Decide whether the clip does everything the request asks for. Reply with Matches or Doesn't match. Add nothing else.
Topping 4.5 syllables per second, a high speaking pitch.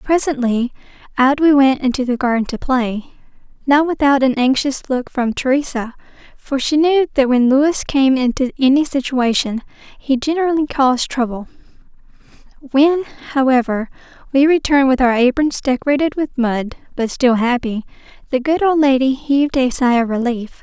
Matches